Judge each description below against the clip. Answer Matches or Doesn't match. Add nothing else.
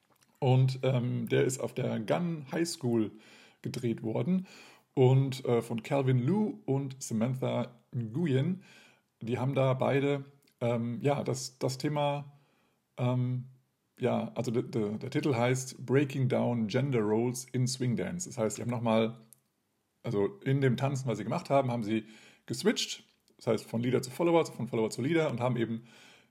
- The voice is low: Matches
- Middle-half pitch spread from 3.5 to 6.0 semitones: Doesn't match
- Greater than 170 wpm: Doesn't match